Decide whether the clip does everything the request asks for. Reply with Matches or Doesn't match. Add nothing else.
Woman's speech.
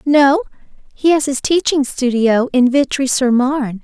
Matches